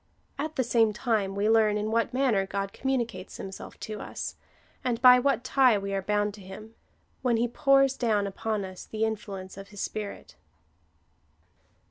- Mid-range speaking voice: No, high, 215 Hz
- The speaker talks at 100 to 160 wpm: No, average, 180 wpm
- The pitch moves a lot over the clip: No, average, 3.4 semitones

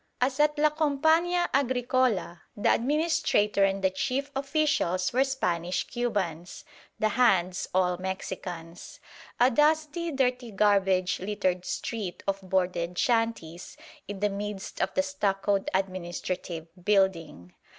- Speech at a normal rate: No, slow, 115 wpm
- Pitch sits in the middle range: No, high, 205 Hz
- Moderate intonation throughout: No, wide, 6.3 semitones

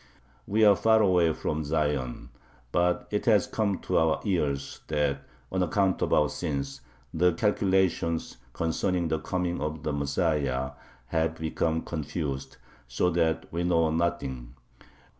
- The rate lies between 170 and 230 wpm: No, average, 140 wpm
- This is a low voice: Yes, very low, 80 Hz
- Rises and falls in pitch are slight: No, average, 3.5 semitones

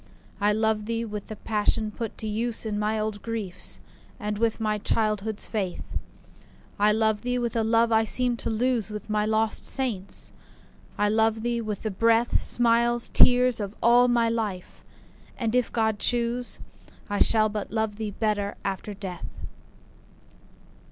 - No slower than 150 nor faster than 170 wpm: Yes, average, 155 wpm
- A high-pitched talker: Yes, high, 220 Hz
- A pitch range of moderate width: No, narrow, 1.7 semitones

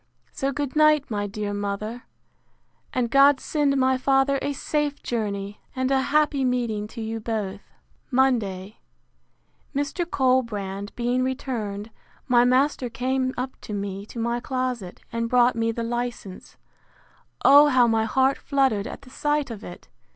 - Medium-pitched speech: No, high, 245 Hz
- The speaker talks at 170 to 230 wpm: No, average, 150 wpm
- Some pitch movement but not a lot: Yes, average, 3.8 semitones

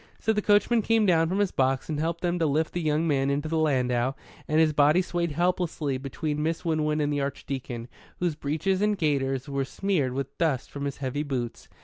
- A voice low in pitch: No, medium, 150 Hz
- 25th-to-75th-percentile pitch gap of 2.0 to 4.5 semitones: Yes, average, 3.8 semitones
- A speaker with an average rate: No, fast, 215 wpm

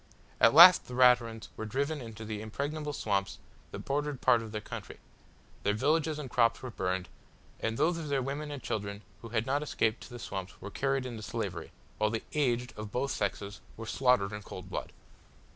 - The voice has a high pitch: No, low, 120 Hz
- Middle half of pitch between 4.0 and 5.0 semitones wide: Yes, average, 4.6 semitones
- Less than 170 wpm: No, average, 195 wpm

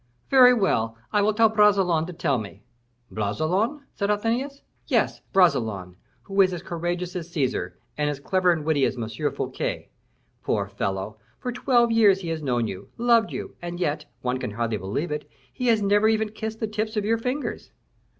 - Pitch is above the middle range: No, medium, 180 Hz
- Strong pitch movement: Yes, wide, 7.8 semitones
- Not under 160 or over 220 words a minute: Yes, average, 185 wpm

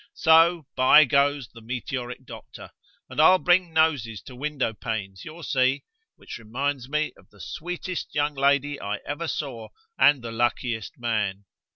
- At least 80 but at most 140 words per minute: No, average, 155 wpm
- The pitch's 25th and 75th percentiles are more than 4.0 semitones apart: Yes, average, 4.6 semitones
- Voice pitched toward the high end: No, low, 135 Hz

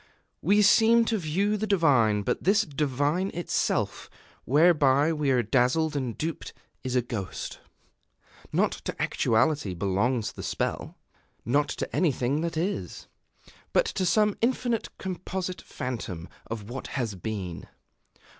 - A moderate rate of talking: No, slow, 130 wpm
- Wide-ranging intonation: Yes, wide, 7.3 semitones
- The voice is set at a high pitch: No, medium, 145 Hz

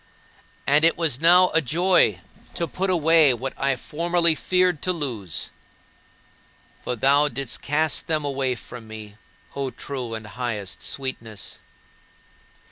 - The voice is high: No, medium, 140 Hz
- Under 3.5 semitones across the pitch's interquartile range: No, average, 5.3 semitones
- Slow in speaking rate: Yes, slow, 130 wpm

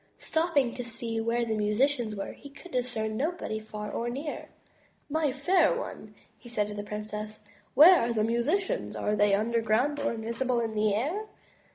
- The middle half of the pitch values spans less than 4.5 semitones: No, average, 4.9 semitones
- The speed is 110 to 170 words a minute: No, average, 185 wpm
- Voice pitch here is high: Yes, high, 235 Hz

